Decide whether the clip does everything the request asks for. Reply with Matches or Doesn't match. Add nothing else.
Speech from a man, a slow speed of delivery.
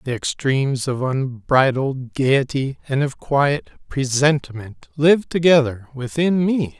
Matches